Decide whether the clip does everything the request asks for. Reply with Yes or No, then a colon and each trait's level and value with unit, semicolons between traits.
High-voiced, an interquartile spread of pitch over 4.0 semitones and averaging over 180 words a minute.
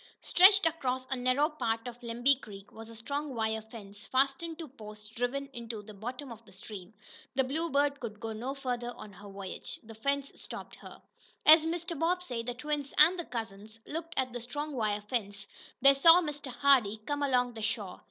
Yes: high, 245 Hz; average, 4.5 semitones; average, 190 wpm